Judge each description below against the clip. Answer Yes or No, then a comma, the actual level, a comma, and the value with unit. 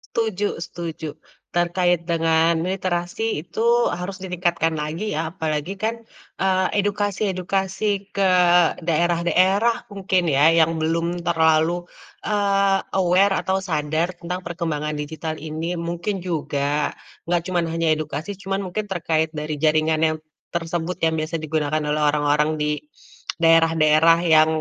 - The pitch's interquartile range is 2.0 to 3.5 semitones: Yes, average, 3.0 semitones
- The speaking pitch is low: No, medium, 170 Hz